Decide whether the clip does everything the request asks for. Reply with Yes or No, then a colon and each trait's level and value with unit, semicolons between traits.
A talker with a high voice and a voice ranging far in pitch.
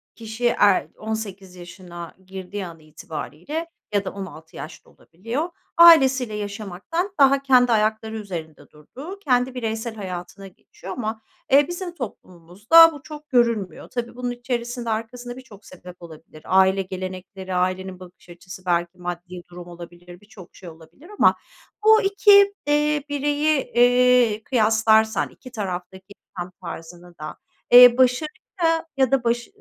Yes: high, 215 Hz; wide, 5.7 semitones